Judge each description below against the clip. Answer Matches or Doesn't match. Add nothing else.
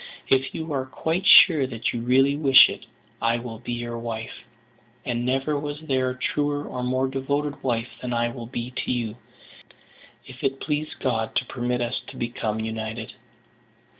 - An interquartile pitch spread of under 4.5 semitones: Matches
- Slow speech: Doesn't match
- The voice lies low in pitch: Matches